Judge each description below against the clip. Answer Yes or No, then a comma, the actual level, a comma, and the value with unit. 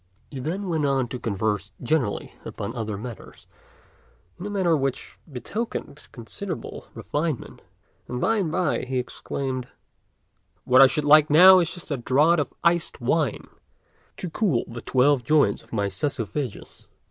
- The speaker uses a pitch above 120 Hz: Yes, medium, 140 Hz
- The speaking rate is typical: Yes, average, 150 wpm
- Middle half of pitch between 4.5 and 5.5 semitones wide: Yes, average, 5.2 semitones